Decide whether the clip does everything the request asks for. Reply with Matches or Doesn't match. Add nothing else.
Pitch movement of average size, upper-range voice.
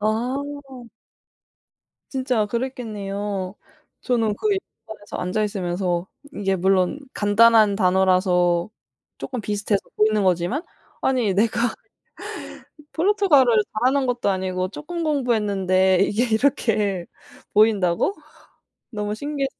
Matches